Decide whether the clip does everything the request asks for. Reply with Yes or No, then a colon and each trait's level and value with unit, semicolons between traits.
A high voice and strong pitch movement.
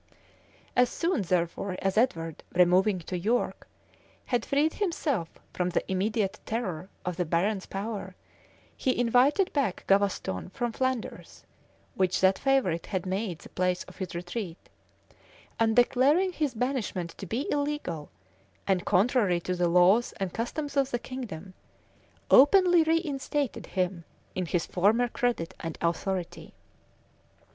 Yes: high, 200 Hz; wide, 6.1 semitones